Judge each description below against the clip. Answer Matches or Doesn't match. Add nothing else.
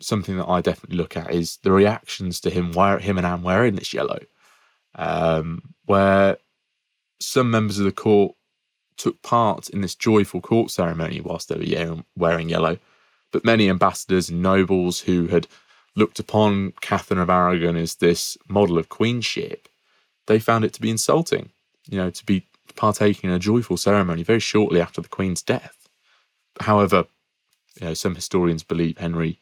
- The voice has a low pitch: Matches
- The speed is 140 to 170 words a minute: Matches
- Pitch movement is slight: Doesn't match